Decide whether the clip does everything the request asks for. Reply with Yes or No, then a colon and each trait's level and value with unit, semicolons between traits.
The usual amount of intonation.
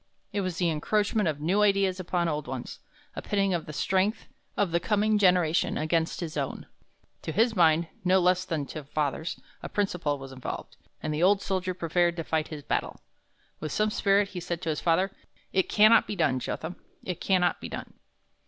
Yes: average, 3.8 semitones